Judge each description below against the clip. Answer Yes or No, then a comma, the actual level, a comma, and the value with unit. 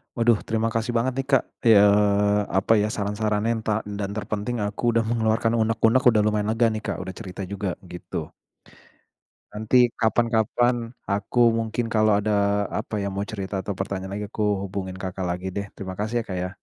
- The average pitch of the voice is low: Yes, low, 105 Hz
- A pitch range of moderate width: No, narrow, 2.2 semitones